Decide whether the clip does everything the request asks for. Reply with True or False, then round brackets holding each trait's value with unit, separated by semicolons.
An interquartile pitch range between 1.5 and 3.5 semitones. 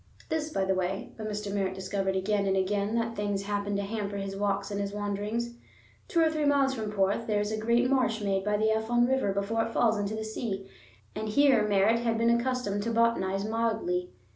True (2.6 semitones)